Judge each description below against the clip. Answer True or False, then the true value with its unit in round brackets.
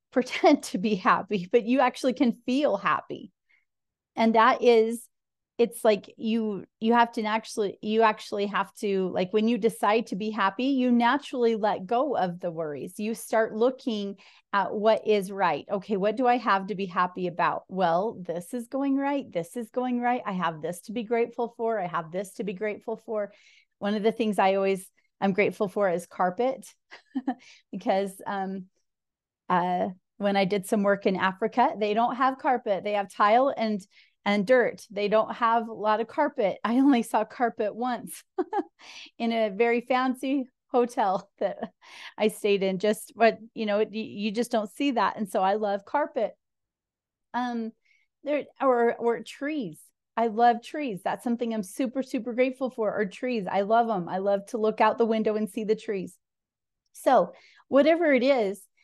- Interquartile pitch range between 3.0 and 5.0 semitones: True (3.3 semitones)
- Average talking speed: True (180 wpm)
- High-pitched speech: True (225 Hz)